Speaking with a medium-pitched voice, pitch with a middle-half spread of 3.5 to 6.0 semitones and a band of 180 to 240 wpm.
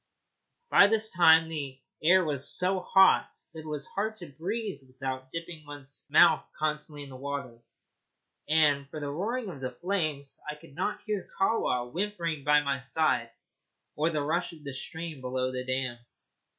No: medium, 150 Hz; average, 4.1 semitones; average, 170 wpm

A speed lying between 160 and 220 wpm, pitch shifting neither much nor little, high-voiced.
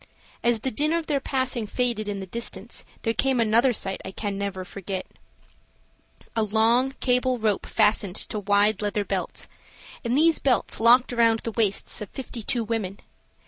Yes: average, 170 wpm; average, 3.4 semitones; high, 225 Hz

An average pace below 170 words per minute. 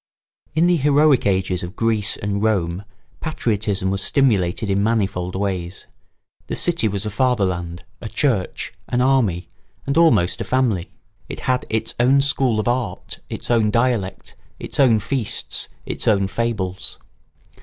Yes: average, 150 wpm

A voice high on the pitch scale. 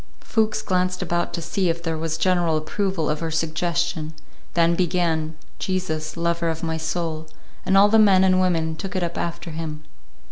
No: medium, 170 Hz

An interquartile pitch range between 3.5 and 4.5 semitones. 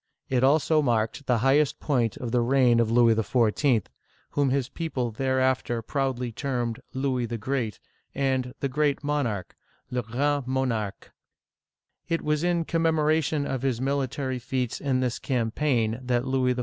No: average, 2.8 semitones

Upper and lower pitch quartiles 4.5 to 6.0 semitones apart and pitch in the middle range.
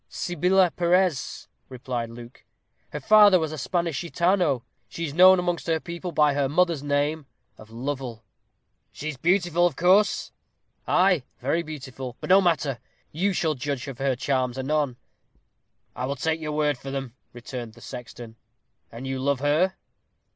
Yes: average, 4.8 semitones; medium, 145 Hz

